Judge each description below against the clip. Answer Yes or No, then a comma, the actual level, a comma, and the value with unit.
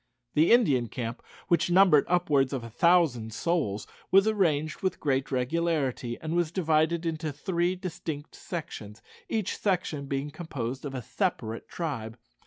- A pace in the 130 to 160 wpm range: Yes, average, 145 wpm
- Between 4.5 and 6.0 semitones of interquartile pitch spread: Yes, average, 4.9 semitones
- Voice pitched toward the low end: No, medium, 155 Hz